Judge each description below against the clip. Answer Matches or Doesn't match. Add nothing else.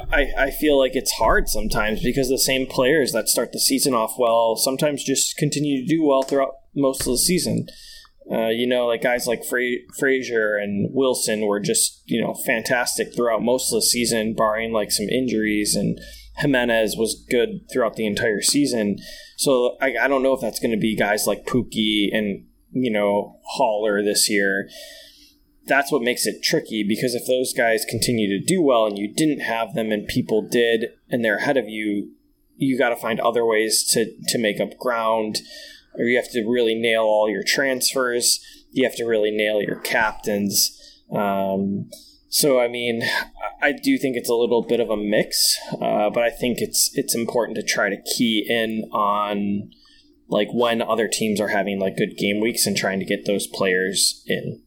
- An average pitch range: Matches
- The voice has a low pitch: Matches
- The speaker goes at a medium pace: Matches